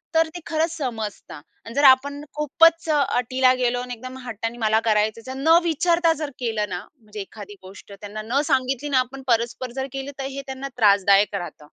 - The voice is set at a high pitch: Yes, very high, 255 Hz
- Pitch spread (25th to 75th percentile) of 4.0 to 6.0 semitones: Yes, average, 4.4 semitones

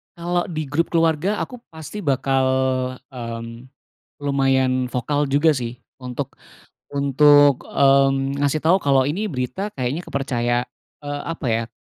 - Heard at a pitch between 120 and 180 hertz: Yes, medium, 140 Hz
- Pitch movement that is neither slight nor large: Yes, average, 3.3 semitones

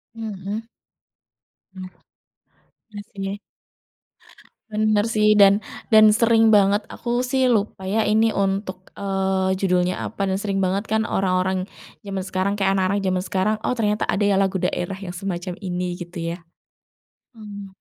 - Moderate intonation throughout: No, narrow, 2.1 semitones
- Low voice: No, high, 195 Hz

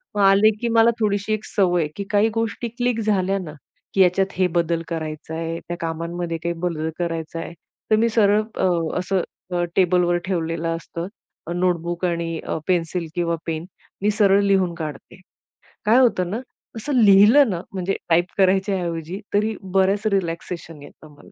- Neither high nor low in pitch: Yes, medium, 180 Hz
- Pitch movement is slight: No, average, 3.3 semitones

